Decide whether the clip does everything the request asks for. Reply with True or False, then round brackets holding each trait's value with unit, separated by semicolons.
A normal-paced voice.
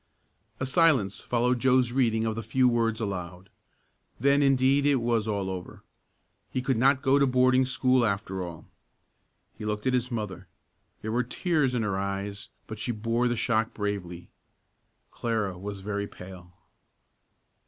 True (155 wpm)